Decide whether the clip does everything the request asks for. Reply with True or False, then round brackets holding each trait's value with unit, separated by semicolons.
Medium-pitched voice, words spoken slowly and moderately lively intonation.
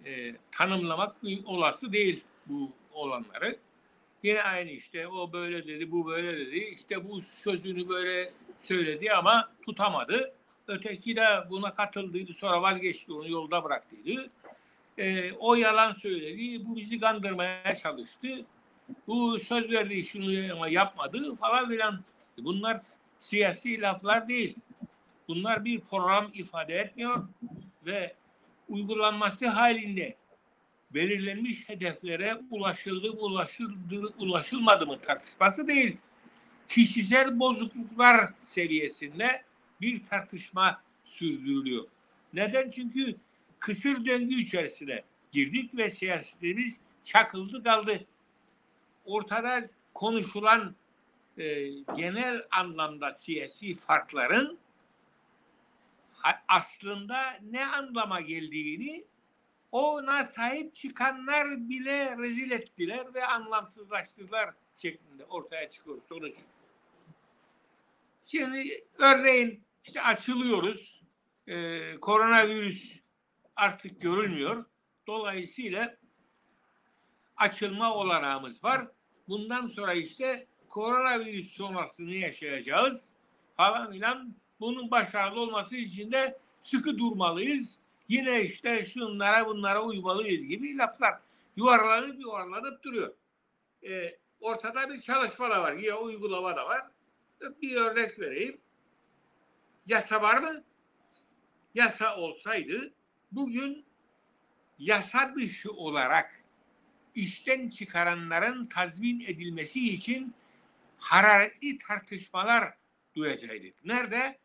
False (220 Hz; 90 wpm; 4.7 semitones)